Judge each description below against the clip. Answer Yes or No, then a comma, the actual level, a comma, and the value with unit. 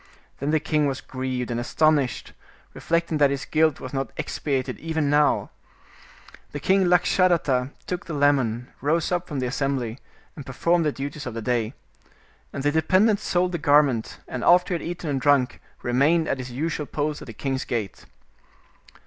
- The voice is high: No, medium, 145 Hz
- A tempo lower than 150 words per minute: No, average, 175 wpm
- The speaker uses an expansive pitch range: No, average, 3.8 semitones